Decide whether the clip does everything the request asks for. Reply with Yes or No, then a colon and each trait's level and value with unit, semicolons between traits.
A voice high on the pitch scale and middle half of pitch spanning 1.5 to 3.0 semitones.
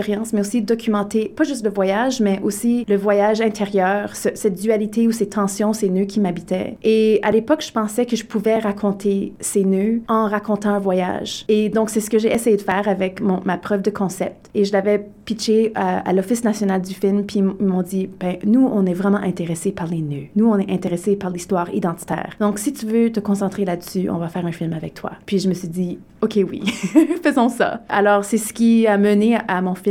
Yes: high, 205 Hz; narrow, 2.6 semitones